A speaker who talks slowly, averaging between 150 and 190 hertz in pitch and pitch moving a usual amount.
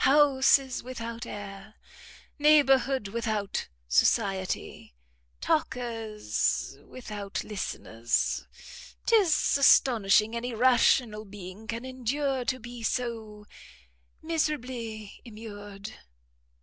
No: slow, 75 wpm; high, 230 Hz; average, 3.7 semitones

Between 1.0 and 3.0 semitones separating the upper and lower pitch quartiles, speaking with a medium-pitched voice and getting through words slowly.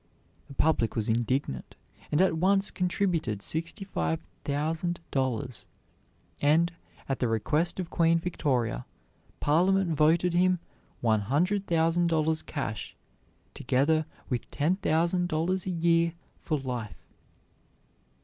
No: average, 4.8 semitones; medium, 160 Hz; slow, 120 wpm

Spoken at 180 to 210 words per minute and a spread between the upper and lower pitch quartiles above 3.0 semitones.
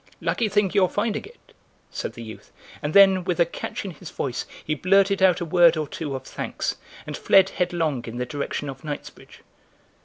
Yes: average, 195 wpm; average, 4.8 semitones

